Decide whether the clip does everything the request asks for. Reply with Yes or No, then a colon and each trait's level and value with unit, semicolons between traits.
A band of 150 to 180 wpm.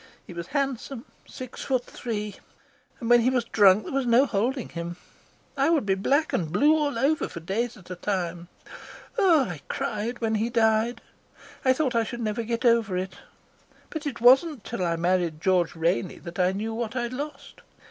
No: average, 190 wpm